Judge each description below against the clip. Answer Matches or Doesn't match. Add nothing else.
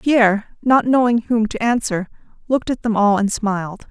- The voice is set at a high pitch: Matches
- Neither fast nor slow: Matches